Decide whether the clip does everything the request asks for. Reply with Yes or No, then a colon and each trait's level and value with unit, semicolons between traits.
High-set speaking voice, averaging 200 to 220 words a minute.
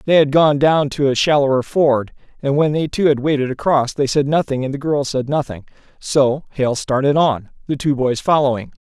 No: medium, 140 Hz; fast, 205 wpm